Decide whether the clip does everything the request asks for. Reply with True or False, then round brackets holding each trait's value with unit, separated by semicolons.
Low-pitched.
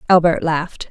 False (165 Hz)